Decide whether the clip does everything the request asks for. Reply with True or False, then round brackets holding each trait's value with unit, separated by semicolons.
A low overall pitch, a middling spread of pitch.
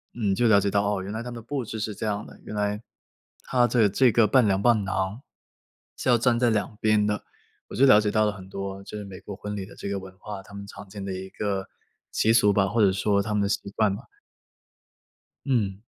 False (105 Hz; 2.2 semitones)